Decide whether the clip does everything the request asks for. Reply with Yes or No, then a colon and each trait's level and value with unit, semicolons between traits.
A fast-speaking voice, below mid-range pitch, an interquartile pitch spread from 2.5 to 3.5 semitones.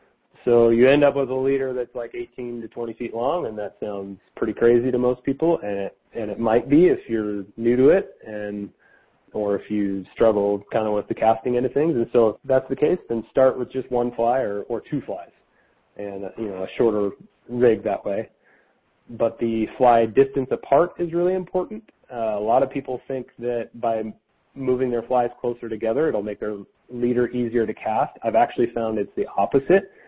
Yes: fast, 210 wpm; low, 120 Hz; average, 3.0 semitones